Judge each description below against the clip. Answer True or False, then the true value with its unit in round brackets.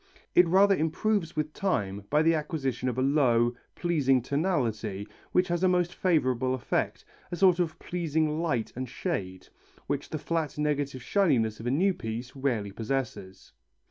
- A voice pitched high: False (145 Hz)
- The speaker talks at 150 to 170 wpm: True (160 wpm)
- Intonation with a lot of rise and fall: True (5.8 semitones)